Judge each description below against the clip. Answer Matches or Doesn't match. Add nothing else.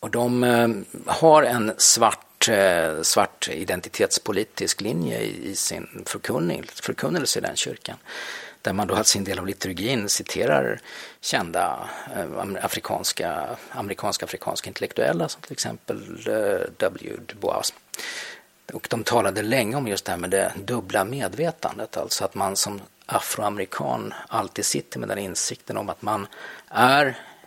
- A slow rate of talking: Matches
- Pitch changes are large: Matches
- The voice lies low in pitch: Matches